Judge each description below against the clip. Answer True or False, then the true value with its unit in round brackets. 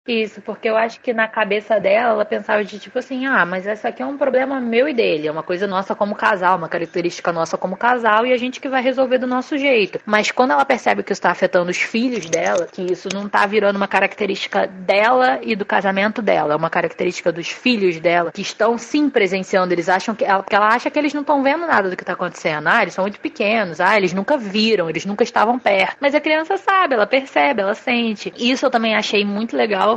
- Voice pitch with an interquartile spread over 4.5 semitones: True (5.0 semitones)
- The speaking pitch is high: True (215 Hz)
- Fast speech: True (240 wpm)